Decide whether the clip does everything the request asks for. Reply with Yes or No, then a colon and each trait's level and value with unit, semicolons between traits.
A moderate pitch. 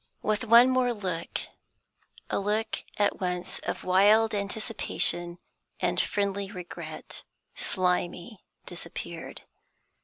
No: high, 200 Hz